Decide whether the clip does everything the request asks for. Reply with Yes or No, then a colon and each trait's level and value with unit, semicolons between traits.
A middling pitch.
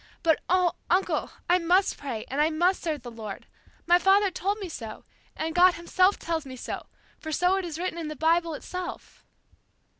No: very high, 340 Hz